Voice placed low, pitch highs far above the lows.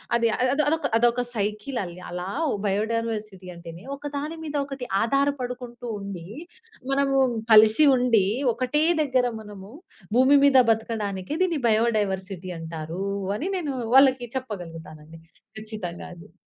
No: high, 225 Hz; wide, 5.8 semitones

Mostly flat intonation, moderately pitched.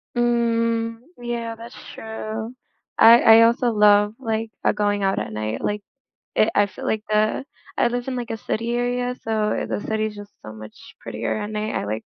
No: narrow, 2.0 semitones; high, 220 Hz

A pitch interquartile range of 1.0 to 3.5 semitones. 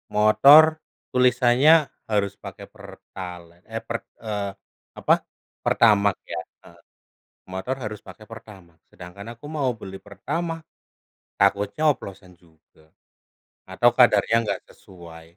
No: average, 4.3 semitones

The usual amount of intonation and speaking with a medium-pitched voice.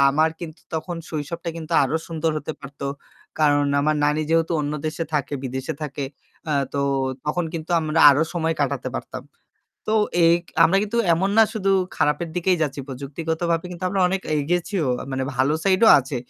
Yes: average, 3.0 semitones; medium, 160 Hz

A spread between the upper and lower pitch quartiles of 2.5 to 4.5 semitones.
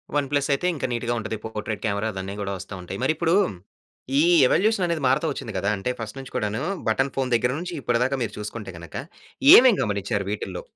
No: average, 5.3 semitones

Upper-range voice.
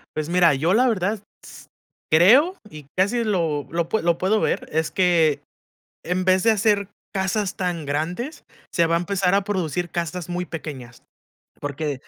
No: medium, 180 Hz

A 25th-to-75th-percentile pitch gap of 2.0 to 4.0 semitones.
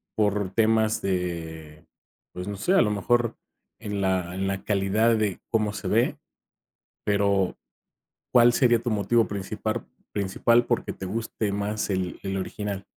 Yes: narrow, 2.6 semitones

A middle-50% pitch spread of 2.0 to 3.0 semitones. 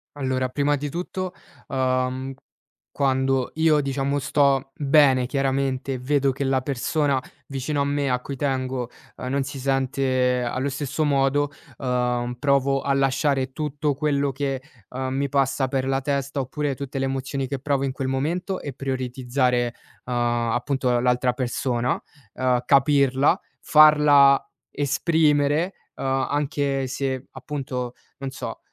No: narrow, 1.6 semitones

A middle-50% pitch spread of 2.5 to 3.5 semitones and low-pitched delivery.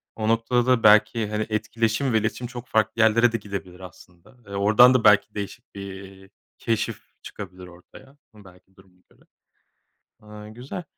Yes: average, 2.9 semitones; low, 105 Hz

